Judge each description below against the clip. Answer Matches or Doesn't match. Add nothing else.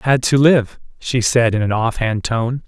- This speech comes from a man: Matches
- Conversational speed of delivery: Doesn't match